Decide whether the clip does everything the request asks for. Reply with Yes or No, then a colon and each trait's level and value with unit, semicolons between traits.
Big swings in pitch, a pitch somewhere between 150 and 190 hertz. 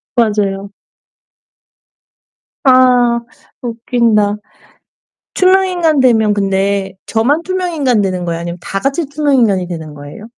No: wide, 5.9 semitones; high, 225 Hz